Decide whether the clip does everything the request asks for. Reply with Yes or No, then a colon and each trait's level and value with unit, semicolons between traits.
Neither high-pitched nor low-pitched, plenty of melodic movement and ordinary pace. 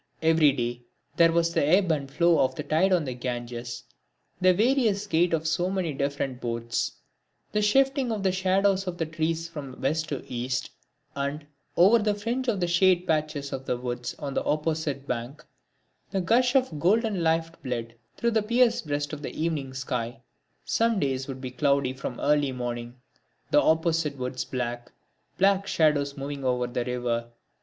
Yes: medium, 155 Hz; wide, 6.0 semitones; average, 175 wpm